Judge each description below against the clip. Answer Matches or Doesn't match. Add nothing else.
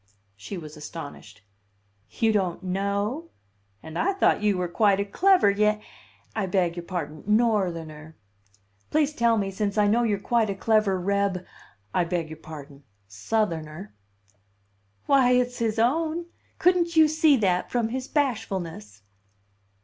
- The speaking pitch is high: Matches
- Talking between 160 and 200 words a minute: Doesn't match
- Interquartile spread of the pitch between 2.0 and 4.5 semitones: Doesn't match